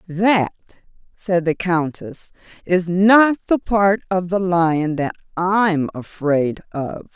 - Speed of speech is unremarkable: No, slow, 125 wpm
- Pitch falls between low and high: Yes, medium, 180 Hz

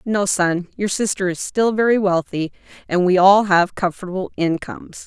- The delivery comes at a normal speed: Yes, average, 165 wpm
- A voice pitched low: No, high, 190 Hz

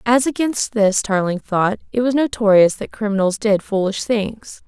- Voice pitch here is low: No, high, 215 Hz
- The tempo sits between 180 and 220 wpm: No, average, 165 wpm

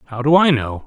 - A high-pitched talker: No, low, 135 Hz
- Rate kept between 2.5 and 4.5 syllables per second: No, 6.2 syllables/s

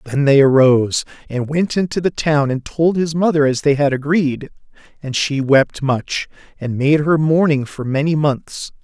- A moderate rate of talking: Yes, average, 185 wpm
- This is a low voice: No, medium, 145 Hz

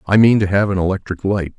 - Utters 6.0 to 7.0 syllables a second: Yes, 6.2 syllables/s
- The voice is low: Yes, low, 100 Hz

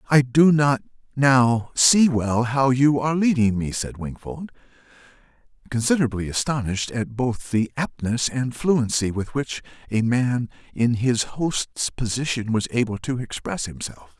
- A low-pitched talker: Yes, low, 125 Hz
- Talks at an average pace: Yes, average, 145 wpm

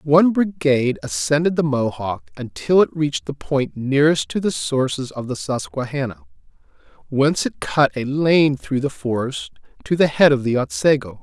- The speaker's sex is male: Yes, male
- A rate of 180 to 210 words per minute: No, average, 165 wpm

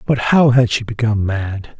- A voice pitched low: Yes, low, 115 Hz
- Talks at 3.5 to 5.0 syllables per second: Yes, 4.9 syllables/s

